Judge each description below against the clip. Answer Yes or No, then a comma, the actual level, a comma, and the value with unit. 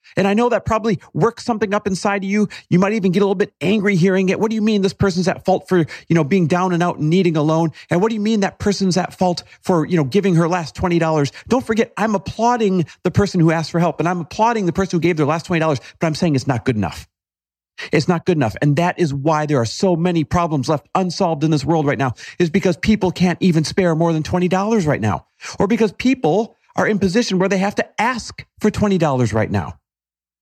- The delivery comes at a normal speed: No, fast, 255 wpm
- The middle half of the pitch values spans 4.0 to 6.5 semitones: Yes, average, 4.3 semitones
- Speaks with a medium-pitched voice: Yes, medium, 180 Hz